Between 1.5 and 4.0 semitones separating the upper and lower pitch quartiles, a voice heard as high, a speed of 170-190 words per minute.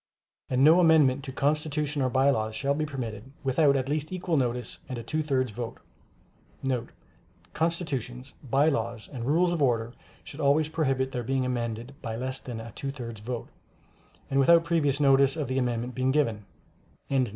No: average, 3.5 semitones; low, 135 Hz; average, 175 wpm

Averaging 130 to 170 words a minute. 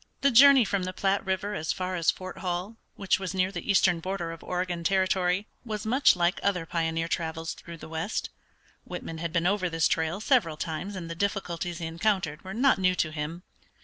No: fast, 205 wpm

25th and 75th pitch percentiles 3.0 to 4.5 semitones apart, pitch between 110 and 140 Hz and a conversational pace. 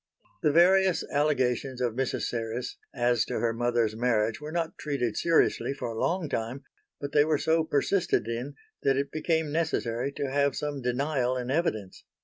Yes: average, 4.0 semitones; low, 135 Hz; average, 170 wpm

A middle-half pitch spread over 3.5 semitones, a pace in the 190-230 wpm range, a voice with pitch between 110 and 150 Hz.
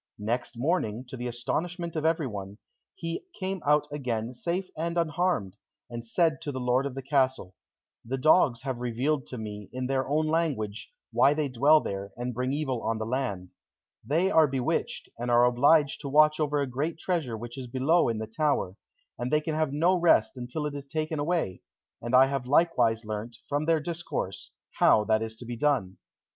Yes: average, 4.7 semitones; average, 195 wpm; low, 135 Hz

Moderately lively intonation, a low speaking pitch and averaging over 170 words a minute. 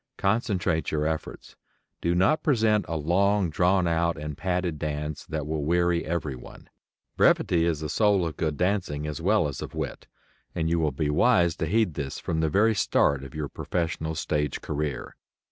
Yes: average, 3.2 semitones; very low, 80 Hz; average, 180 wpm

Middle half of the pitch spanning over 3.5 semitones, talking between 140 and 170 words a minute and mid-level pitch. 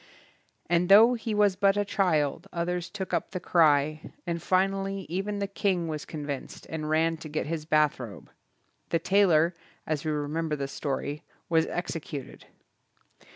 Yes: average, 4.0 semitones; average, 155 wpm; medium, 165 Hz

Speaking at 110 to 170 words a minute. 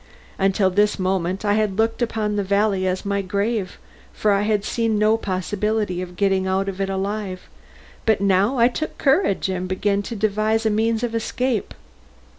No: average, 180 wpm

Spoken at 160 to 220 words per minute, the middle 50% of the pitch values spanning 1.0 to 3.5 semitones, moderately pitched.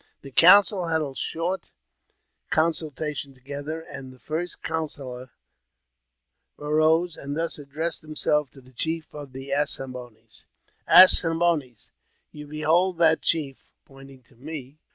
No: average, 140 wpm; average, 3.2 semitones; medium, 150 Hz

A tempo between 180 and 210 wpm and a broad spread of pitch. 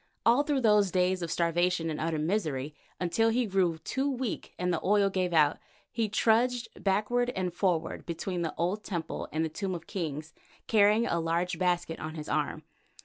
No: average, 185 wpm; average, 4.3 semitones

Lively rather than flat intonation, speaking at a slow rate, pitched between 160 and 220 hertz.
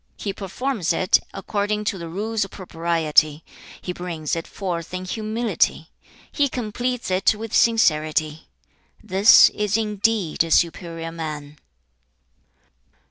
No: average, 4.5 semitones; slow, 120 wpm; medium, 185 Hz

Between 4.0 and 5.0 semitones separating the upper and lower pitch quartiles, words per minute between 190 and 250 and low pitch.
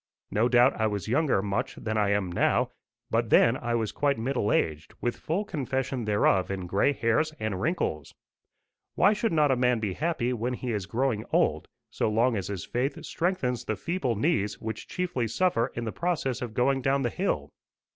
Yes: average, 4.4 semitones; average, 195 wpm; low, 120 Hz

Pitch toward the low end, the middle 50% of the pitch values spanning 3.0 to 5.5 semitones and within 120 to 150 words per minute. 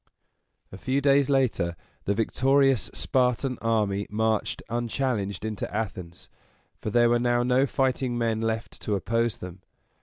Yes: low, 115 Hz; average, 3.4 semitones; average, 140 wpm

